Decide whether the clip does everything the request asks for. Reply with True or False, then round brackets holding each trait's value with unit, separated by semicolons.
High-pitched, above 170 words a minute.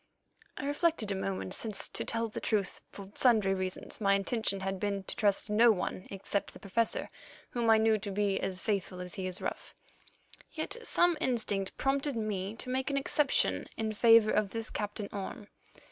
True (210 Hz; 185 wpm)